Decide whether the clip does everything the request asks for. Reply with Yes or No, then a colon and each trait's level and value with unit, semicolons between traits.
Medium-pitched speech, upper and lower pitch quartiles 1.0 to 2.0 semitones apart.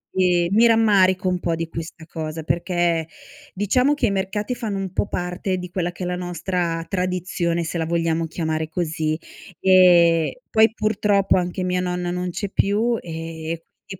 No: medium, 180 Hz; narrow, 2.4 semitones